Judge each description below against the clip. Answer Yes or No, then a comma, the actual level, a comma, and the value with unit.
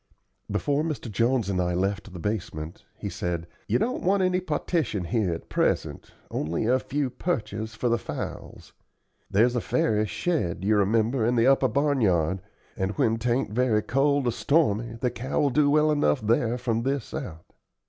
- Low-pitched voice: Yes, low, 115 Hz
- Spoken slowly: No, average, 175 wpm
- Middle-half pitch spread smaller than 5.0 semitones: No, average, 5.3 semitones